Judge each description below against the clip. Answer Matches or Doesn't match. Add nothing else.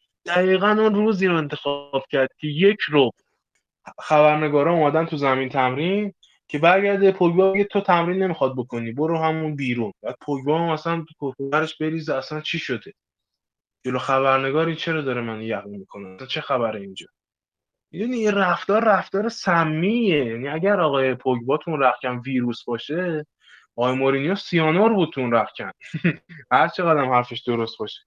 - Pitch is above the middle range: Doesn't match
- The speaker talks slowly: Doesn't match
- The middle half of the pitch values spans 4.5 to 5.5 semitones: Matches